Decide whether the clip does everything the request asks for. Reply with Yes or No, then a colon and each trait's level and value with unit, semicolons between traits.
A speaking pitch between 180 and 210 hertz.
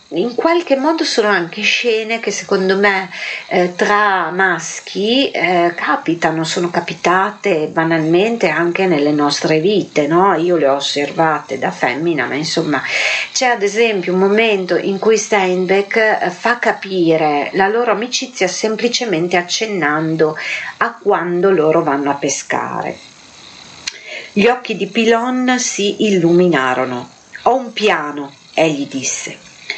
Yes: high, 190 Hz